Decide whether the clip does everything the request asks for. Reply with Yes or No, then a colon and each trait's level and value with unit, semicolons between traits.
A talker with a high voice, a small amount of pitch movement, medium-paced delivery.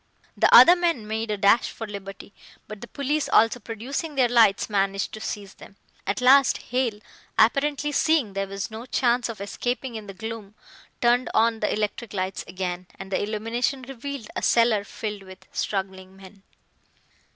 No: high, 220 Hz; average, 3.8 semitones; average, 170 wpm